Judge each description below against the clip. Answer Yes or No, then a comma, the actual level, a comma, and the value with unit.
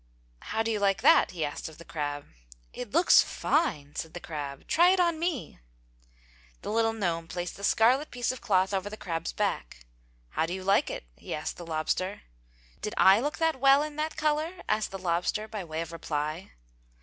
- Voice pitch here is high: Yes, high, 195 Hz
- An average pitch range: No, wide, 7.7 semitones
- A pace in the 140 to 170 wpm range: No, average, 200 wpm